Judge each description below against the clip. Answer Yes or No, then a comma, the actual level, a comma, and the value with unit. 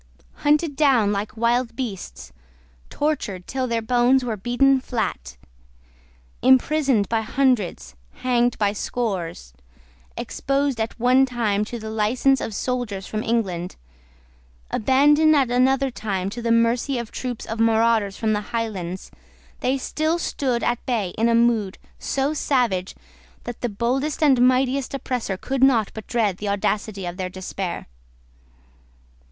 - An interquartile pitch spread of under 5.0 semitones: Yes, average, 4.0 semitones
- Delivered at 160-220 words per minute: No, average, 140 wpm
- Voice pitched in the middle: No, high, 235 Hz